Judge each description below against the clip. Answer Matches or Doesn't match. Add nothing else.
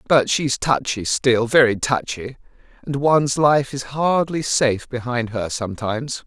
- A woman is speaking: Doesn't match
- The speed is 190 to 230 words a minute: Doesn't match